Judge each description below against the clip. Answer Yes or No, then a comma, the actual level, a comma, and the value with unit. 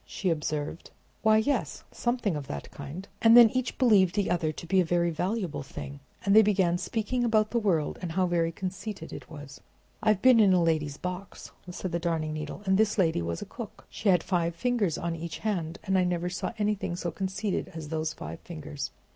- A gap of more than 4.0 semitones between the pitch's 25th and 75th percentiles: Yes, average, 4.5 semitones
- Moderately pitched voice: Yes, medium, 180 Hz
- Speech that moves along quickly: Yes, fast, 215 wpm